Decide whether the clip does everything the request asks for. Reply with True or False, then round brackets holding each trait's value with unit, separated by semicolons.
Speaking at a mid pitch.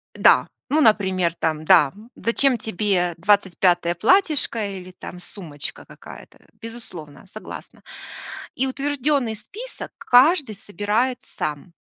False (205 Hz)